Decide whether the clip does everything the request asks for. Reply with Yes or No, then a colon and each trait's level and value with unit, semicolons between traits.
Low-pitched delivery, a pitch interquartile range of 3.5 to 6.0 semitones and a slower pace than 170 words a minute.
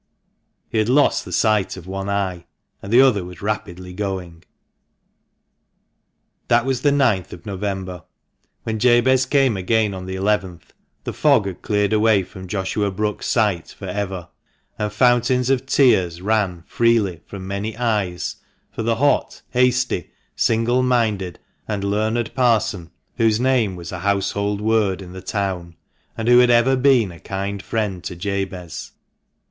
Yes: low, 105 Hz; average, 3.8 semitones; average, 155 wpm